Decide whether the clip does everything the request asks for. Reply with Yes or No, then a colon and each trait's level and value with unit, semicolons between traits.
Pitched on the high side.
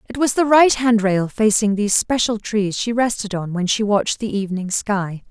Yes: high, 215 Hz